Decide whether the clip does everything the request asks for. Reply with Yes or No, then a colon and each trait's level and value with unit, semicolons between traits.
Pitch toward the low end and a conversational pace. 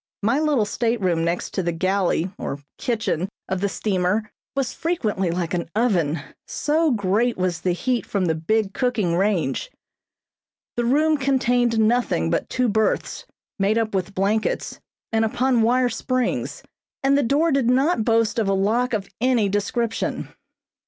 No: high, 220 Hz; average, 150 wpm